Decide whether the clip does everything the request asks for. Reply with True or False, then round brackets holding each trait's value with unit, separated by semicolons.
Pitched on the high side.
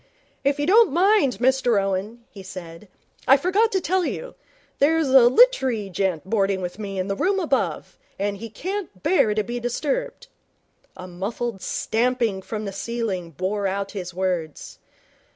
True (220 Hz)